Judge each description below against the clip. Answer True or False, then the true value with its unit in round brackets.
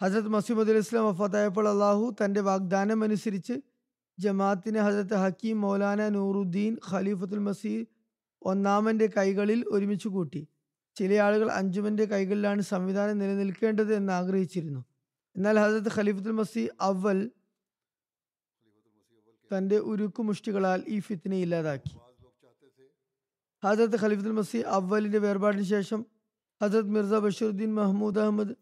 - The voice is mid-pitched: False (205 Hz)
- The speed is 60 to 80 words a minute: False (100 wpm)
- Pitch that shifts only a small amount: True (1.9 semitones)